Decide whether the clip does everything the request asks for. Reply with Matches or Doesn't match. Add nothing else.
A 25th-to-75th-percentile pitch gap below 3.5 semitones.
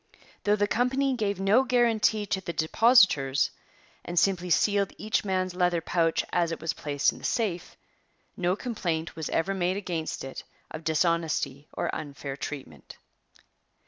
Doesn't match